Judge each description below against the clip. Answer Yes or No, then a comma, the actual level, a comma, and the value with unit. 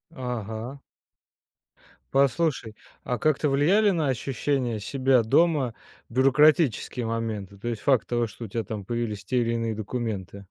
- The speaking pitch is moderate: No, low, 120 Hz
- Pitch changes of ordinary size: Yes, average, 3.6 semitones